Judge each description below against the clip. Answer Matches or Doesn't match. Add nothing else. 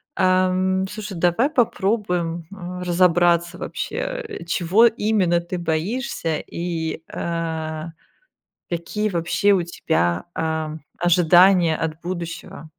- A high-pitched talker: Doesn't match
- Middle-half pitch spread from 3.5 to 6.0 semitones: Doesn't match